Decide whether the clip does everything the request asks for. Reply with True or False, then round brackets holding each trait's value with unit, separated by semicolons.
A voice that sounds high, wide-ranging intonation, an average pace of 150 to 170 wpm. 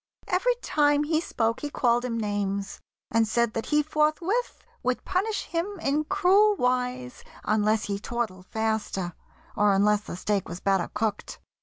True (235 Hz; 6.6 semitones; 155 wpm)